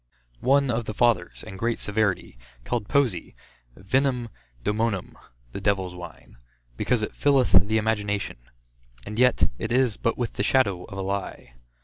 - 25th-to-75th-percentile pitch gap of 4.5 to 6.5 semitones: No, average, 3.8 semitones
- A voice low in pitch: Yes, low, 110 Hz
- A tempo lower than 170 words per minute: Yes, average, 150 wpm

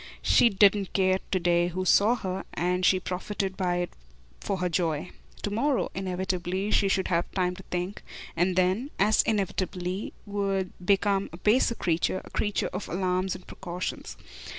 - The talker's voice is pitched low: No, medium, 185 Hz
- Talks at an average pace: Yes, average, 165 wpm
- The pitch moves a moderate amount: No, narrow, 1.8 semitones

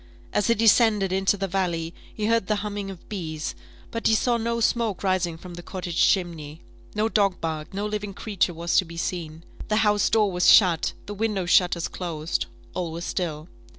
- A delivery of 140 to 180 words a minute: No, average, 190 wpm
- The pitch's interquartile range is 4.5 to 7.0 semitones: No, average, 3.7 semitones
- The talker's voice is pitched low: No, high, 190 Hz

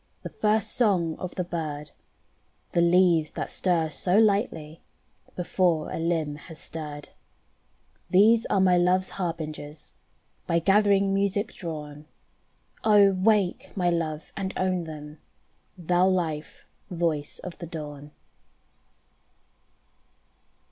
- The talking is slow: Yes, slow, 115 wpm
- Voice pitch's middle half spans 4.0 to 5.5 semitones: No, average, 3.4 semitones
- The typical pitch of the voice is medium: Yes, medium, 175 Hz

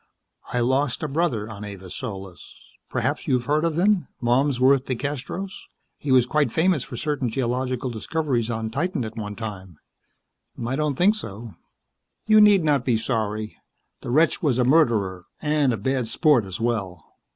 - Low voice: Yes, low, 125 Hz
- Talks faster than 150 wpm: Yes, average, 165 wpm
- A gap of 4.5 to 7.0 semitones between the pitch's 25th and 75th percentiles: Yes, average, 5.2 semitones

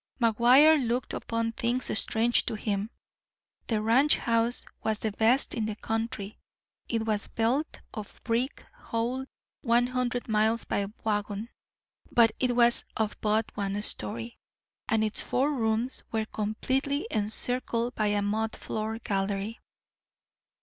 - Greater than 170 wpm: No, slow, 135 wpm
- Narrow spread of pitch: Yes, narrow, 2.2 semitones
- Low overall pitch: No, high, 225 Hz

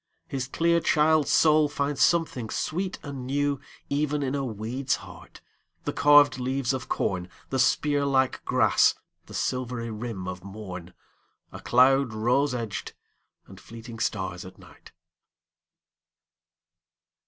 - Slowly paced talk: Yes, slow, 120 wpm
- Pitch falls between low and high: No, low, 130 Hz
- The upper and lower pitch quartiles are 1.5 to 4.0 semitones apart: No, average, 4.5 semitones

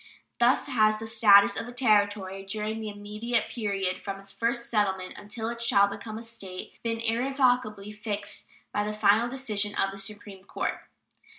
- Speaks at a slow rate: No, average, 170 wpm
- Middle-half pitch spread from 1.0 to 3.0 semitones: Yes, narrow, 2.4 semitones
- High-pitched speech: Yes, high, 210 Hz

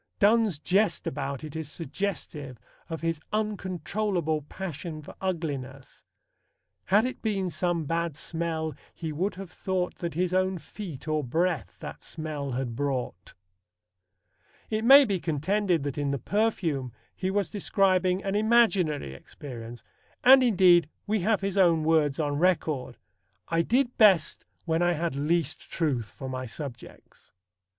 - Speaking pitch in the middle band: Yes, medium, 170 Hz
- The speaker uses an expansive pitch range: No, average, 4.9 semitones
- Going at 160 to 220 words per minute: No, average, 145 wpm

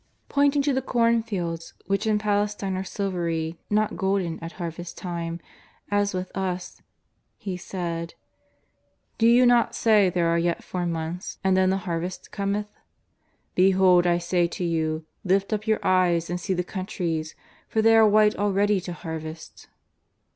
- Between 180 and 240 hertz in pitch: Yes, medium, 185 Hz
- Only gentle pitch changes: No, average, 3.3 semitones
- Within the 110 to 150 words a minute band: No, average, 160 wpm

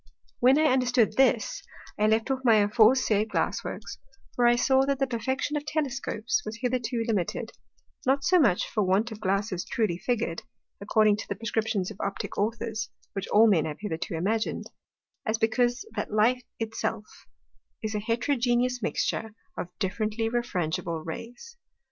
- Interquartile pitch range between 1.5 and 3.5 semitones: Yes, average, 3.1 semitones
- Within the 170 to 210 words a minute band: No, average, 160 wpm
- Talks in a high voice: Yes, high, 225 Hz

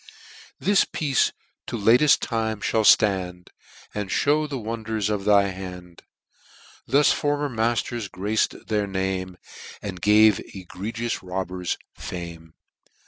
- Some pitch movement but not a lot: Yes, average, 3.8 semitones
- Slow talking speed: Yes, slow, 115 wpm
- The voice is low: Yes, low, 105 Hz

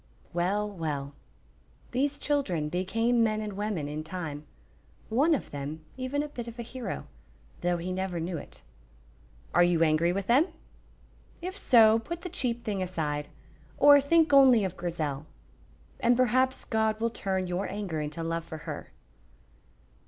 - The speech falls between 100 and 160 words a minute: Yes, average, 155 wpm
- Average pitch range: No, wide, 6.6 semitones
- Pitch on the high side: Yes, high, 195 Hz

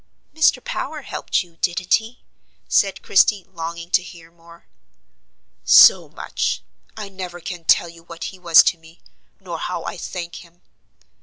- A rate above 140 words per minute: Yes, average, 155 wpm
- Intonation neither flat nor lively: No, narrow, 1.9 semitones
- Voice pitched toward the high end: No, medium, 175 Hz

